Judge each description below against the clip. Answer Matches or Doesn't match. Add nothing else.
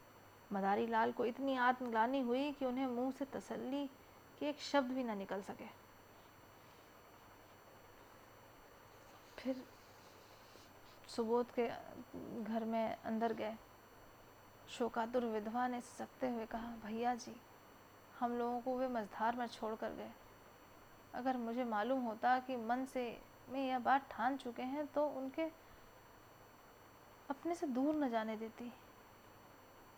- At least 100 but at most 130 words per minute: Matches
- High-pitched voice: Matches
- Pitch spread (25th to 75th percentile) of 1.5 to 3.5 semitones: Matches